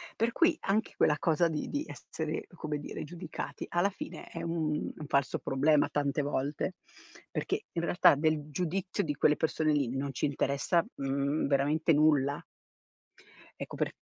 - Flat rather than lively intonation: No, average, 3.1 semitones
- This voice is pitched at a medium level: Yes, medium, 150 Hz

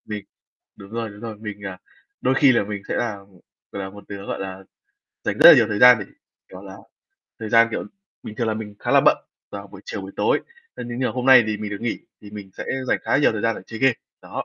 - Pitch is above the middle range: No, low, 105 Hz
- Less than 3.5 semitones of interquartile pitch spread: Yes, narrow, 2.6 semitones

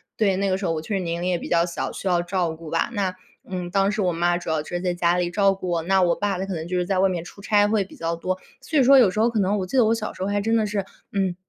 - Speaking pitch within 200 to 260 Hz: No, medium, 185 Hz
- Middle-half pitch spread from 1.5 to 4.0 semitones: Yes, narrow, 2.5 semitones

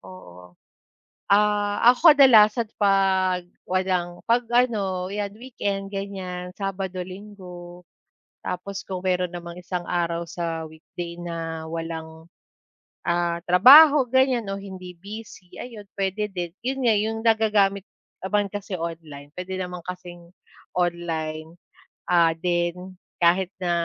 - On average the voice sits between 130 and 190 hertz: Yes, medium, 185 Hz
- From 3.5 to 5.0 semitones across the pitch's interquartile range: No, average, 3.0 semitones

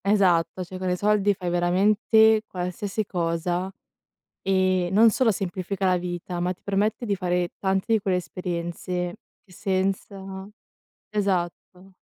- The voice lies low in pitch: No, medium, 185 Hz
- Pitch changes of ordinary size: No, narrow, 2.1 semitones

